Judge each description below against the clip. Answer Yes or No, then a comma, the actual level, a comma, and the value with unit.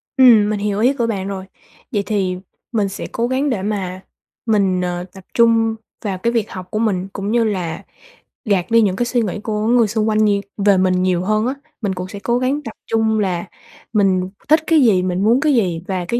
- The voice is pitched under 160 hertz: No, high, 210 Hz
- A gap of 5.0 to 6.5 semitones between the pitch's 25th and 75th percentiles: No, average, 3.5 semitones